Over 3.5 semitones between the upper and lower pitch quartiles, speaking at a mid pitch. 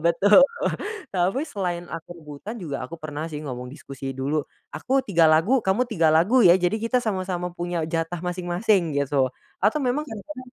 Yes: average, 5.1 semitones; medium, 175 Hz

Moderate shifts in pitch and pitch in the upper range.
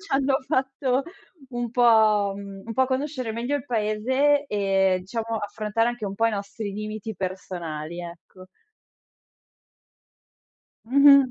Yes: average, 4.6 semitones; high, 225 Hz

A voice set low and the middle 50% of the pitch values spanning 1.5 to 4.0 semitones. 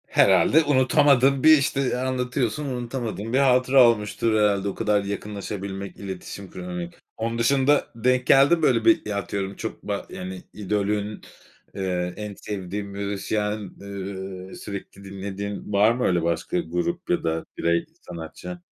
No: low, 105 Hz; average, 4.6 semitones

